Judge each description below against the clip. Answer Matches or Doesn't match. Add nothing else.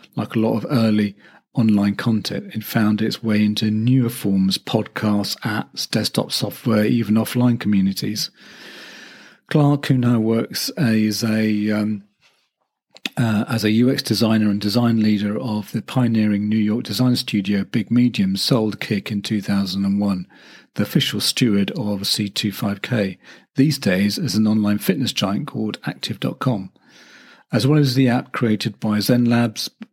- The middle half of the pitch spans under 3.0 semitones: Matches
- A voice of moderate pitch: Doesn't match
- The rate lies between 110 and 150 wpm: Matches